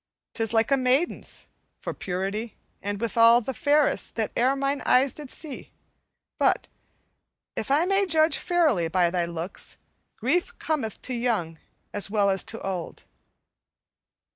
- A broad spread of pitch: Yes, wide, 6.3 semitones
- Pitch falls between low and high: No, high, 235 Hz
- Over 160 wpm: No, average, 140 wpm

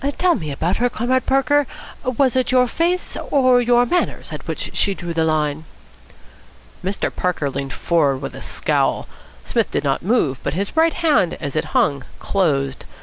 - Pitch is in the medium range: No, high, 195 Hz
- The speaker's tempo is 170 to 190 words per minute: Yes, average, 175 wpm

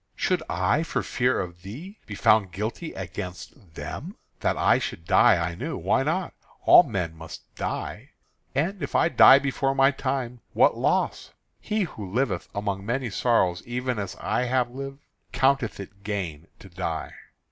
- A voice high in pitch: No, low, 115 Hz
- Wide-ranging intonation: Yes, wide, 6.3 semitones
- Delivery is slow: No, average, 165 wpm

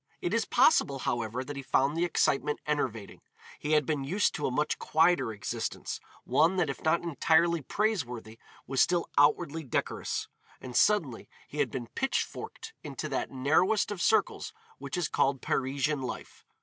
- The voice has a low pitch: No, medium, 150 Hz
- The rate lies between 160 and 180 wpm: Yes, average, 165 wpm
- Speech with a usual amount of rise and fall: Yes, average, 4.5 semitones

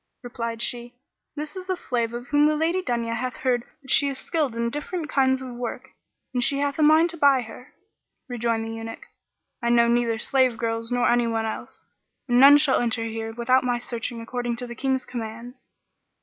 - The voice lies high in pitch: Yes, high, 245 Hz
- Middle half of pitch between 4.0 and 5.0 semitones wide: No, average, 3.0 semitones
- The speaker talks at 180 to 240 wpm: Yes, fast, 205 wpm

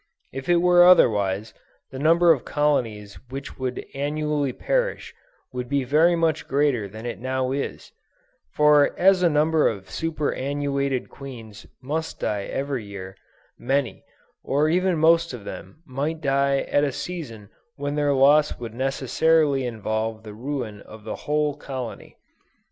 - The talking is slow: No, average, 145 wpm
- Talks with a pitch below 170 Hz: Yes, medium, 140 Hz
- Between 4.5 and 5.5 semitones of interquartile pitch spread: No, average, 4.1 semitones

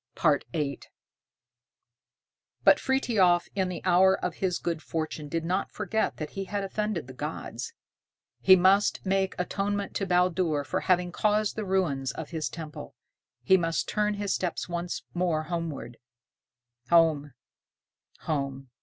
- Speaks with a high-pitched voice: No, medium, 175 Hz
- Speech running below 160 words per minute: Yes, slow, 135 wpm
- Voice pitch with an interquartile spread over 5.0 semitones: No, average, 3.6 semitones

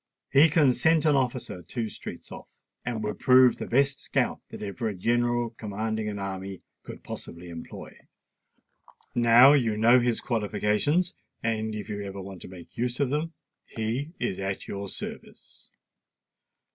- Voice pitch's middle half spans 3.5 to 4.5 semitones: Yes, average, 3.9 semitones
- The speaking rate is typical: Yes, average, 160 wpm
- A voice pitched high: No, low, 115 Hz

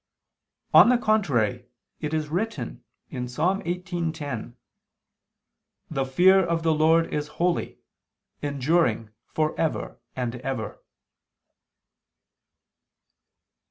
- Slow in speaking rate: Yes, slow, 90 wpm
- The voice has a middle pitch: Yes, medium, 155 Hz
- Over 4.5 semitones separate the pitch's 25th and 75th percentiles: Yes, average, 5.2 semitones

